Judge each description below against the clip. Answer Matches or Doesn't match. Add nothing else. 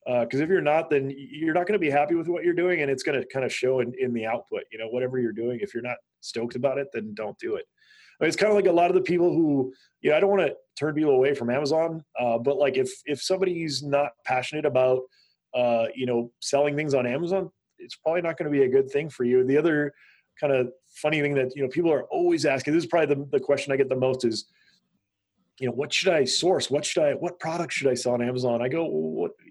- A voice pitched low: Doesn't match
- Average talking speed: Doesn't match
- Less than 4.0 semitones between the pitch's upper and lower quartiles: Doesn't match